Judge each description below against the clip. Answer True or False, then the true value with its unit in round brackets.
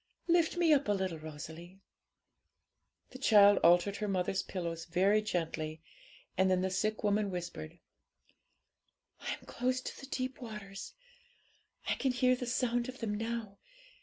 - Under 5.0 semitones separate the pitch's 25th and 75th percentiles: False (5.3 semitones)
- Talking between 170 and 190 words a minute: False (145 wpm)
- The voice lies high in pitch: True (205 Hz)